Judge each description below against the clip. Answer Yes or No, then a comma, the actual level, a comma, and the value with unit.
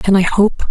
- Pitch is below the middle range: No, high, 195 Hz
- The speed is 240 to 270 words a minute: Yes, fast, 255 wpm